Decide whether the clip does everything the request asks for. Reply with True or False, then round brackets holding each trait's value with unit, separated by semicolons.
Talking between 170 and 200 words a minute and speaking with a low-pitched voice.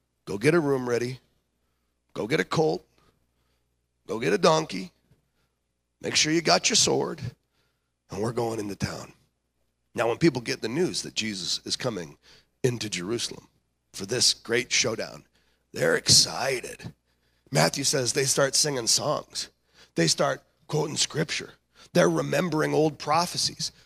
False (140 wpm; 110 Hz)